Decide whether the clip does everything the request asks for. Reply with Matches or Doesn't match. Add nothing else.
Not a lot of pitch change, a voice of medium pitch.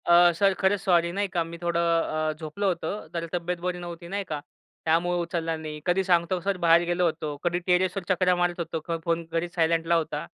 Matches